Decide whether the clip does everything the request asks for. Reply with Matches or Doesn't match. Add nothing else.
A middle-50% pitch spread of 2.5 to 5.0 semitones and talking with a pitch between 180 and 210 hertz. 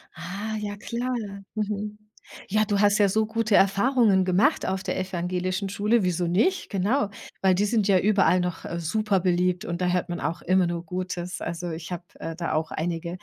Matches